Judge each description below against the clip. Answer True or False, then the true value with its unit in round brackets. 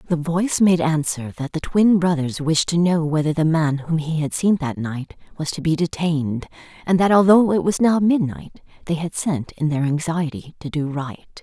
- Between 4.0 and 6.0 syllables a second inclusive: True (4.9 syllables/s)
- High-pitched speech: False (160 Hz)